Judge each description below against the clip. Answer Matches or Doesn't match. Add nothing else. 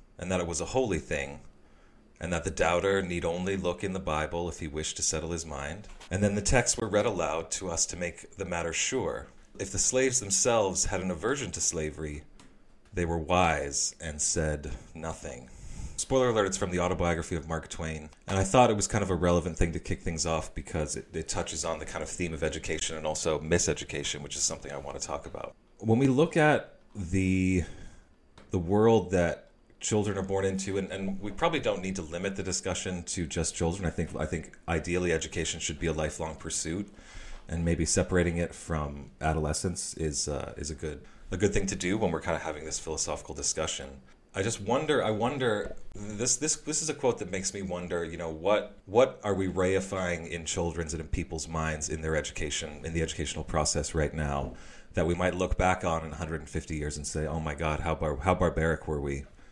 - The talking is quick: Matches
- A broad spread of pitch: Doesn't match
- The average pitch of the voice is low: Matches